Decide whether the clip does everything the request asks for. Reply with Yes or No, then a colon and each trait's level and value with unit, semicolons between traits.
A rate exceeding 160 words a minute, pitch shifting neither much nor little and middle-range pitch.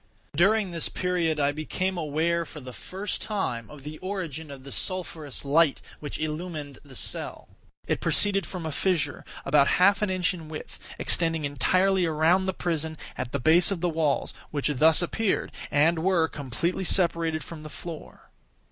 Yes: average, 170 wpm; average, 3.5 semitones; medium, 160 Hz